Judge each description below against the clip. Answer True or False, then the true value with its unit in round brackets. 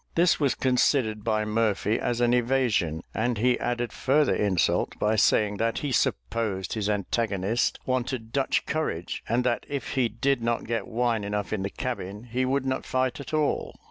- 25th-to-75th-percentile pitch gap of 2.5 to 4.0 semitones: True (3.5 semitones)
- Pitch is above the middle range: False (115 Hz)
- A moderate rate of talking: True (175 wpm)